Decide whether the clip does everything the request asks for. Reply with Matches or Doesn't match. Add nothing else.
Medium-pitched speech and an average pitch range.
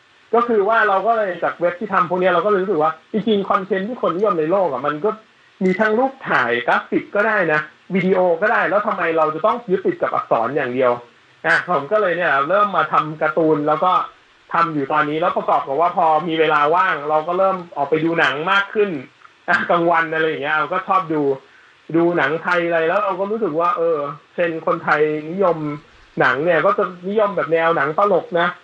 Matches